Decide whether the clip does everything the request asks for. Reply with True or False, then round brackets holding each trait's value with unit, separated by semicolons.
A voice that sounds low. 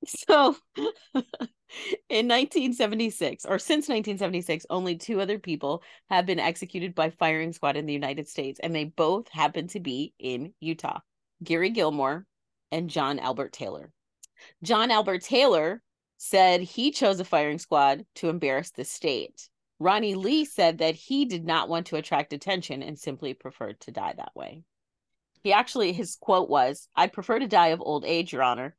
False (175 Hz)